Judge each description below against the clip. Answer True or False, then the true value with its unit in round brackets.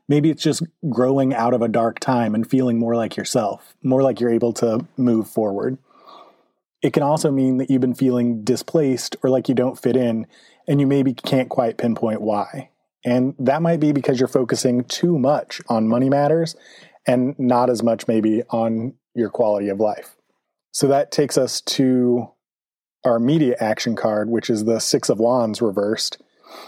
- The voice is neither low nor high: False (125 Hz)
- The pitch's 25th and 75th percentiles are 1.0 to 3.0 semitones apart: True (2.7 semitones)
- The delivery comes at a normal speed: True (180 wpm)